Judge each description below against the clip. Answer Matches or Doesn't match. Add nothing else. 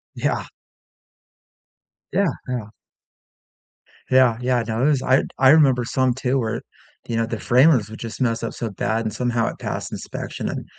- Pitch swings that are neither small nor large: Doesn't match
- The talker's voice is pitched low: Matches